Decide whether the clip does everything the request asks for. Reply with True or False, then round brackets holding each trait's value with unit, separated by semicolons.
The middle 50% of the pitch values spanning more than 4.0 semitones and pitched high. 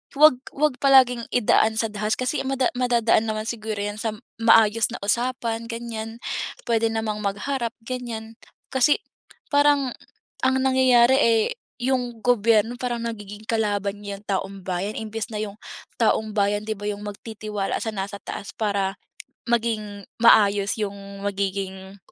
False (2.7 semitones; 220 Hz)